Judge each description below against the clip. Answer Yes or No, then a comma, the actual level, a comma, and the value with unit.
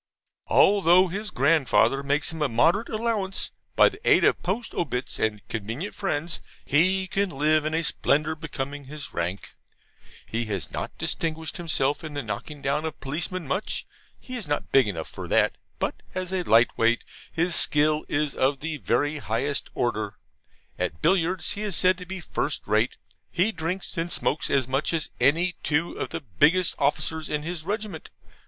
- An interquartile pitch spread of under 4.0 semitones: No, average, 4.8 semitones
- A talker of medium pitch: Yes, medium, 155 Hz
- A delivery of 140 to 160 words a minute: No, average, 175 wpm